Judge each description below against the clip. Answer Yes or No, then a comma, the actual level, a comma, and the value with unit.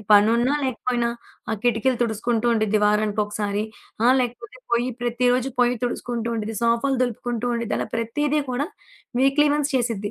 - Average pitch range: No, narrow, 2.2 semitones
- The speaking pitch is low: No, high, 235 Hz